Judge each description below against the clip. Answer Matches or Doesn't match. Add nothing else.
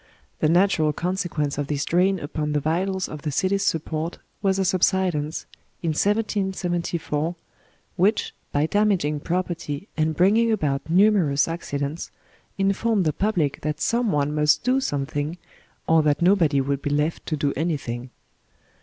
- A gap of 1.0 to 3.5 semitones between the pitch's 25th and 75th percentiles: Doesn't match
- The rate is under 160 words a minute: Matches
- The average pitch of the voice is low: Doesn't match